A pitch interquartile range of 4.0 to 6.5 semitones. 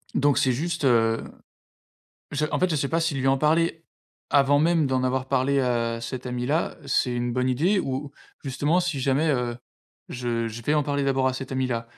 No: average, 3.2 semitones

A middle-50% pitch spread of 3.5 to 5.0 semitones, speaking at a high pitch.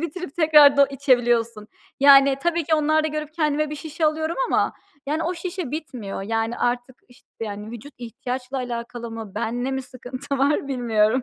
Yes: average, 4.3 semitones; very high, 270 Hz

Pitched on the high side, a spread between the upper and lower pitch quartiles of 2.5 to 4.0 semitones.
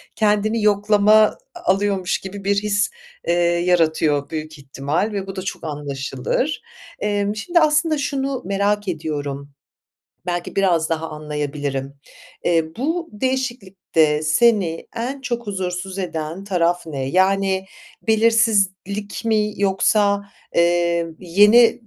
No: high, 195 Hz; average, 4.5 semitones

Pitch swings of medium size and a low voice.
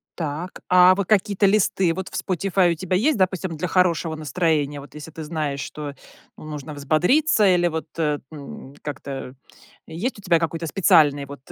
No: average, 3.7 semitones; medium, 165 Hz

